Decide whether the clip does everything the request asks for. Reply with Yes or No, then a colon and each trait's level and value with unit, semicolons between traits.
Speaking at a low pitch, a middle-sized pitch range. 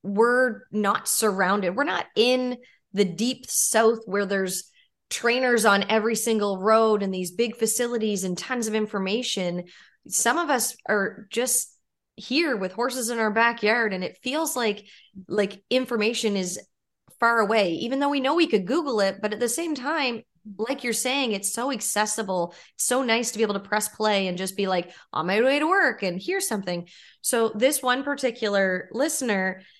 No: high, 220 Hz; average, 3.7 semitones